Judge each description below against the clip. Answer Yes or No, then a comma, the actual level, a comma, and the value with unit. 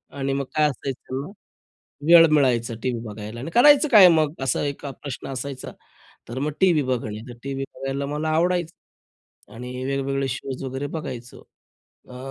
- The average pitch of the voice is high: No, low, 135 Hz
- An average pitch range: Yes, average, 3.2 semitones